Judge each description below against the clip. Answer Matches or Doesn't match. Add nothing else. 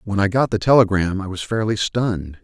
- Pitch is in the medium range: Doesn't match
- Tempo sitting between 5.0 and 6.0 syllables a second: Matches